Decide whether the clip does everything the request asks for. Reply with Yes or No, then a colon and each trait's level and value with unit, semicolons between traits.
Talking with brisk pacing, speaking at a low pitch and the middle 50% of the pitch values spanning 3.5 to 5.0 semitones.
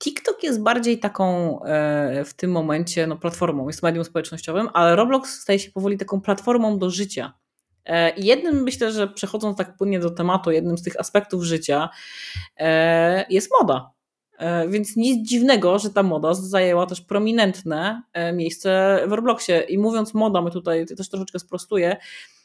No: fast, 165 wpm; medium, 185 Hz; average, 3.9 semitones